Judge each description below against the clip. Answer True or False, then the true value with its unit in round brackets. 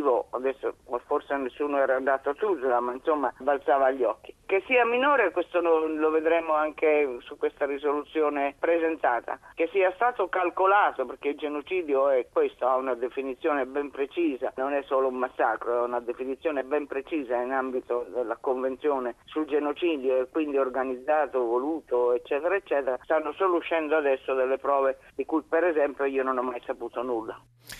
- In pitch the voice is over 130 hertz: True (140 Hz)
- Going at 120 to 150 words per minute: False (160 wpm)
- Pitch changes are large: False (3.7 semitones)